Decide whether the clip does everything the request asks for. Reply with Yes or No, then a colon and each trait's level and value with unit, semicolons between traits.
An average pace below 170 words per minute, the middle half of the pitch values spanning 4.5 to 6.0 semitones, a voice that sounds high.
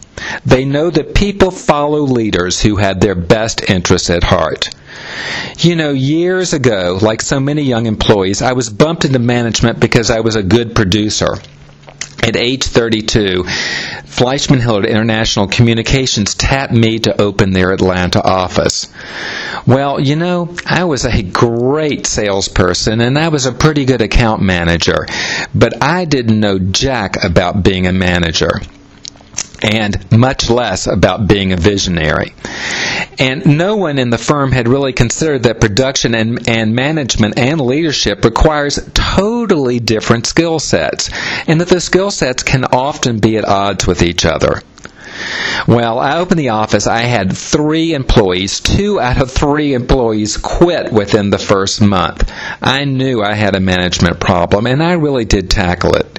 No: average, 155 wpm; wide, 5.5 semitones; low, 115 Hz